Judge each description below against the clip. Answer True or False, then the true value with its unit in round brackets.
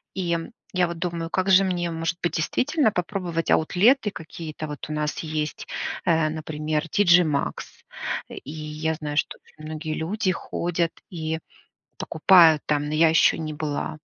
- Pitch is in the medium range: True (165 Hz)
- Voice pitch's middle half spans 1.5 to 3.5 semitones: True (2.5 semitones)